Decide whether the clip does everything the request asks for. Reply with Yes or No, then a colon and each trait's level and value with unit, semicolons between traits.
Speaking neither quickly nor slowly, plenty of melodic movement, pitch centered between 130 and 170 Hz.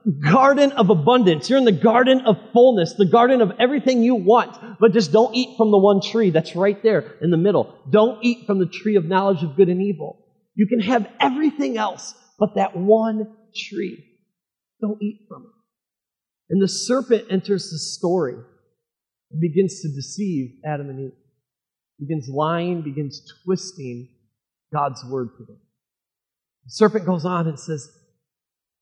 No: average, 165 wpm; wide, 6.2 semitones; high, 195 Hz